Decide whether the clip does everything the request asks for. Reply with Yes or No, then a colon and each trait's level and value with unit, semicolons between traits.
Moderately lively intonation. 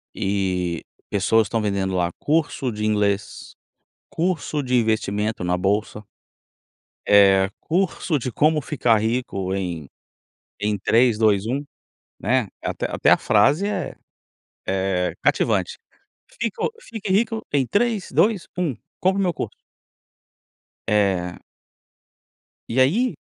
No: wide, 8.1 semitones